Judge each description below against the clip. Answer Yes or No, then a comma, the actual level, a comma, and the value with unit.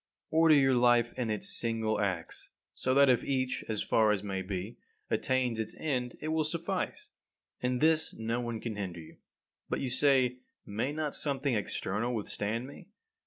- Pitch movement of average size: Yes, average, 3.9 semitones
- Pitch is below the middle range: Yes, low, 125 Hz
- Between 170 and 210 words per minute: Yes, average, 175 wpm